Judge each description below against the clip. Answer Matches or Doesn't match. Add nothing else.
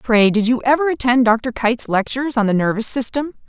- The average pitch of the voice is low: Doesn't match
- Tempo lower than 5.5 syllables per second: Doesn't match